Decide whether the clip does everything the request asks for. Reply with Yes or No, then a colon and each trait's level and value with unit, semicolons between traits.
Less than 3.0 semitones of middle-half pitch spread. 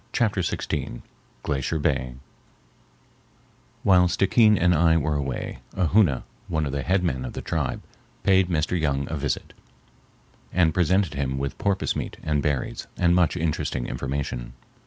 No: average, 4.6 semitones